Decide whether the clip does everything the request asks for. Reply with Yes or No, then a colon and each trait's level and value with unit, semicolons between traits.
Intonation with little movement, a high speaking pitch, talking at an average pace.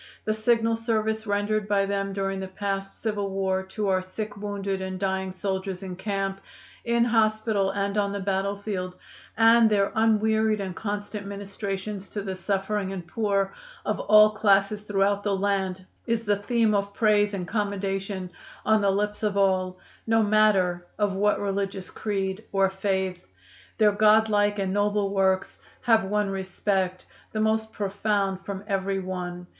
Yes: narrow, 1.7 semitones; high, 200 Hz; average, 160 wpm